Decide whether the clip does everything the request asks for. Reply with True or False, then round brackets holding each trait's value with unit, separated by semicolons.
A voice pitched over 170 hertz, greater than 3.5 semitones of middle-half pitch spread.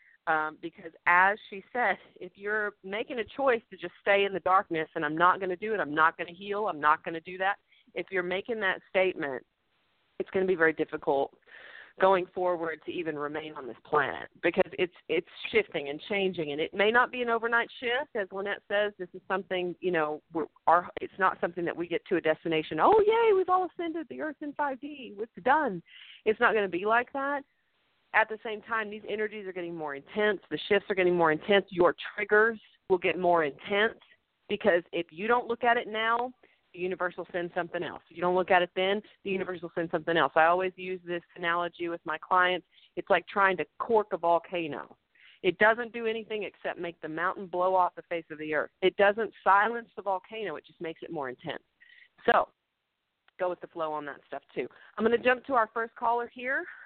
True (190 Hz; 4.4 semitones)